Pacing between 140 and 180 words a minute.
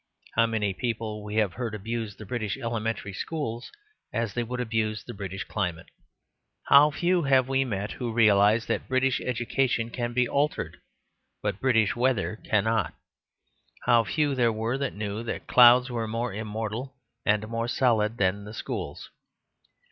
Yes: average, 160 wpm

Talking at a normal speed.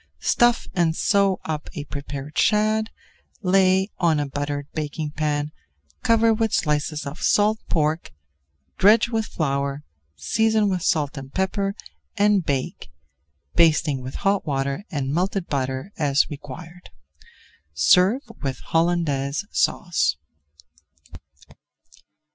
No: slow, 115 wpm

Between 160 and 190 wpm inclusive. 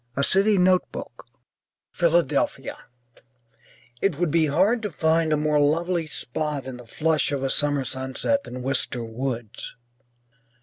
No: slow, 135 wpm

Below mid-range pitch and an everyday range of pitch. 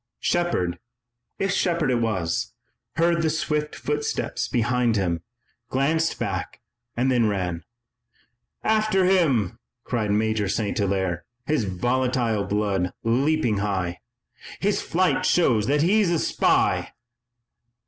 No: low, 120 Hz; wide, 8.0 semitones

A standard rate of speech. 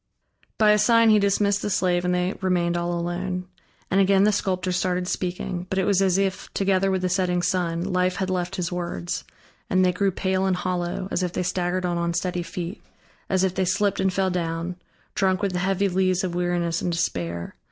No: fast, 210 wpm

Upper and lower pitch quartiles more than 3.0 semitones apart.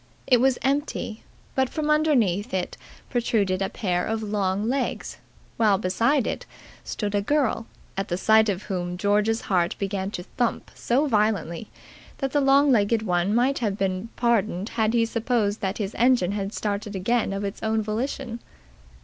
Yes: average, 3.6 semitones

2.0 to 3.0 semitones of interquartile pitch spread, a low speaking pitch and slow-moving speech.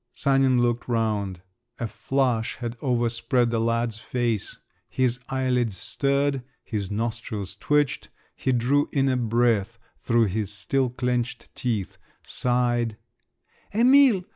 Yes: narrow, 2.5 semitones; low, 120 Hz; slow, 120 wpm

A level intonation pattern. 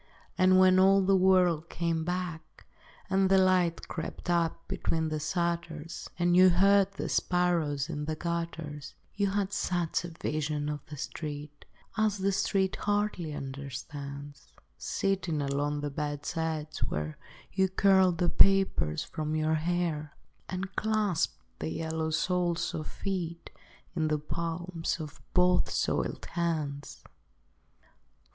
No: average, 3.4 semitones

